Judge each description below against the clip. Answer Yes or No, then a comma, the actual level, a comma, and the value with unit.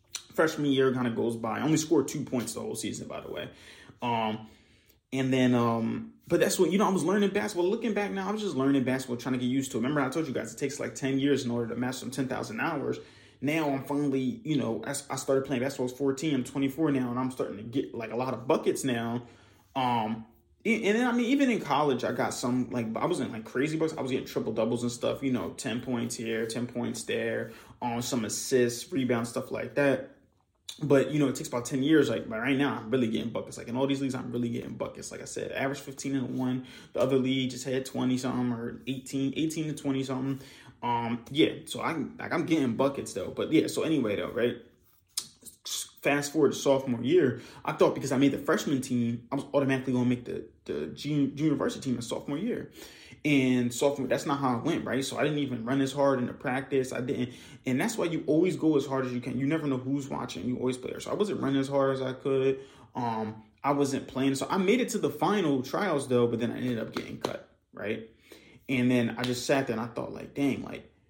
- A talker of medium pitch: No, low, 130 Hz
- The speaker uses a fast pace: Yes, fast, 250 wpm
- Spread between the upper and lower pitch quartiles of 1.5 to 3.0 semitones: Yes, narrow, 2.6 semitones